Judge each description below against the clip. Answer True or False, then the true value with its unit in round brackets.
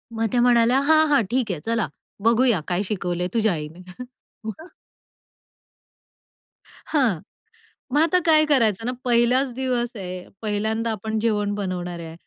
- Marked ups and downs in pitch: False (4.9 semitones)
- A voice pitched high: True (225 Hz)